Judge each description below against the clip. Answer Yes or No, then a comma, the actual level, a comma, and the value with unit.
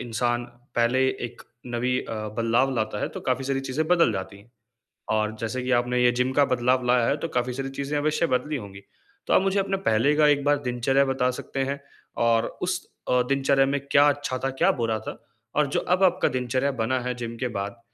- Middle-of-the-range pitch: No, low, 130 Hz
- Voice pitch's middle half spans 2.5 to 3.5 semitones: Yes, average, 3.1 semitones